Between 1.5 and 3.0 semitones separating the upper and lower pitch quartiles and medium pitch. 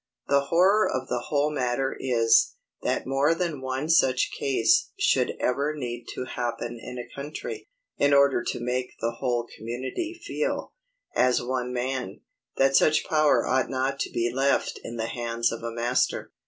No: average, 2.7 semitones; low, 130 Hz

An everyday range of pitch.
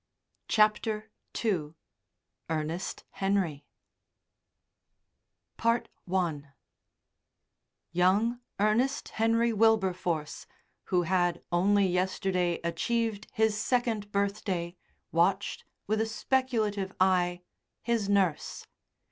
Yes: average, 3.8 semitones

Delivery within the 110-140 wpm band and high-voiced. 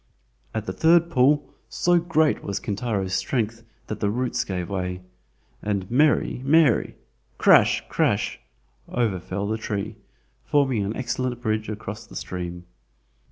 No: slow, 135 wpm; low, 110 Hz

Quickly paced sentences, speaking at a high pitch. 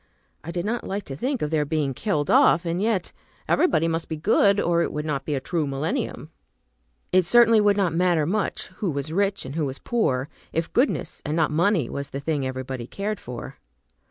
No: fast, 210 wpm; medium, 165 Hz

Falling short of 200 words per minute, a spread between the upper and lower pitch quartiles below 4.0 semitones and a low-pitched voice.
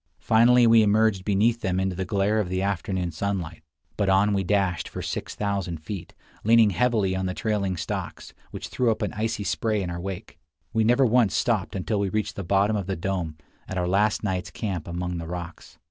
No: fast, 205 wpm; average, 2.9 semitones; low, 100 Hz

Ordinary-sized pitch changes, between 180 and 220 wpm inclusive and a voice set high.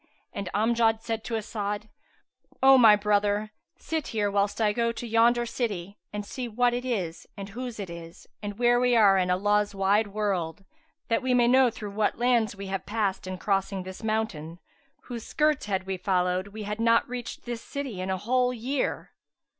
Yes: average, 3.3 semitones; average, 190 wpm; high, 210 Hz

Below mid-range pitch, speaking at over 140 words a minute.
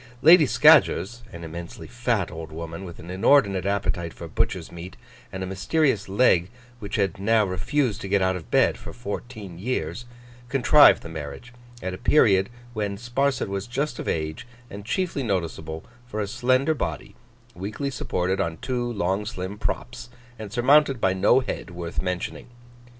Yes: low, 100 Hz; average, 165 wpm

